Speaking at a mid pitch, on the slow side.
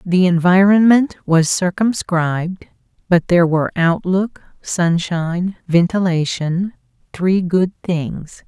Yes: medium, 175 Hz; slow, 85 wpm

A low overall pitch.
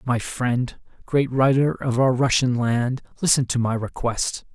Yes: low, 125 Hz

